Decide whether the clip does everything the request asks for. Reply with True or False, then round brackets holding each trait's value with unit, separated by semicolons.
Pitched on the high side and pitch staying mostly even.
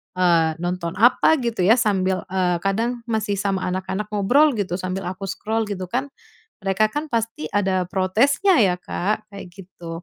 False (195 Hz; 3.4 semitones)